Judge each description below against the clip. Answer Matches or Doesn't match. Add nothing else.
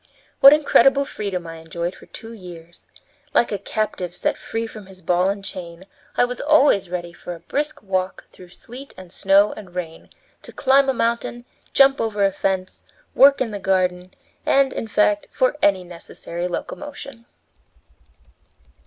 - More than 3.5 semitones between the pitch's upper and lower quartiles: Matches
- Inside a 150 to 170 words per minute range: Matches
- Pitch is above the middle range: Matches